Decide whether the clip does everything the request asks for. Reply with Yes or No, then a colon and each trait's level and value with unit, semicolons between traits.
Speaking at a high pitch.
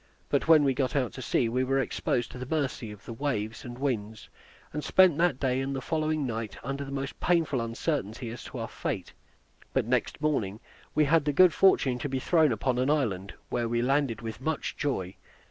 No: low, 130 Hz